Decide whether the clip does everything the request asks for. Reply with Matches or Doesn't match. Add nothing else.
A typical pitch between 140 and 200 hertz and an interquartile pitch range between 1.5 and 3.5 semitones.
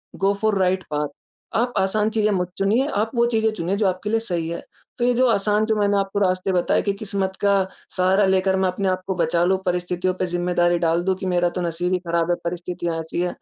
Matches